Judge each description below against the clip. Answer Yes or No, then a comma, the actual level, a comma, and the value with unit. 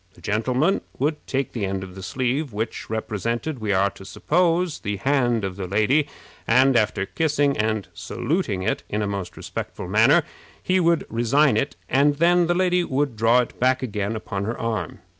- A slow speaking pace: No, average, 185 wpm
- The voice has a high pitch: No, low, 120 Hz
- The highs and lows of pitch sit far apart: Yes, wide, 6.0 semitones